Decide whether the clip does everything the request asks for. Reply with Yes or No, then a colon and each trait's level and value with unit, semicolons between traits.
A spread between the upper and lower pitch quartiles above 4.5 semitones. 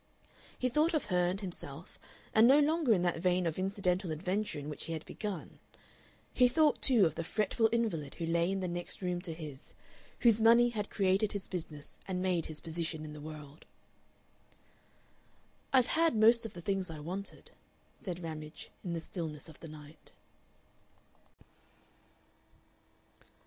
Yes: average, 5.0 semitones